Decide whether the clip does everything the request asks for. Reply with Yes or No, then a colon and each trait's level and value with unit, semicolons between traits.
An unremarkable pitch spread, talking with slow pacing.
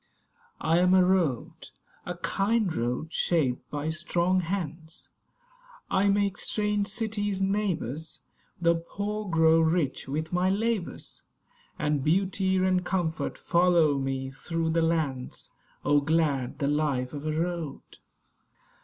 Yes: average, 3.8 semitones; slow, 125 wpm